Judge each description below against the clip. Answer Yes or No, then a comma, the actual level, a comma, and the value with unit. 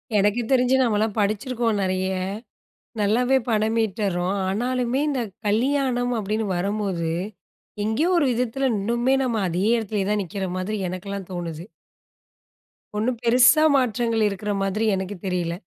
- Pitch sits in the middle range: No, high, 215 Hz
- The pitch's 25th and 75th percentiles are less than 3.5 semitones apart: No, average, 3.9 semitones